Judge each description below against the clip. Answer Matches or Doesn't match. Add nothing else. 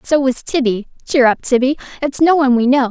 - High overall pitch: Matches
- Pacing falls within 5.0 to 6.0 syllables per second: Matches